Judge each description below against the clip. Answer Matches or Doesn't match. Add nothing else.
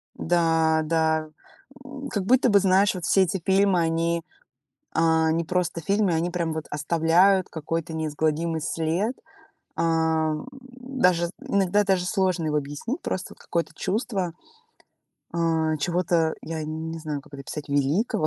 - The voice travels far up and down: Doesn't match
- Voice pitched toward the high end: Doesn't match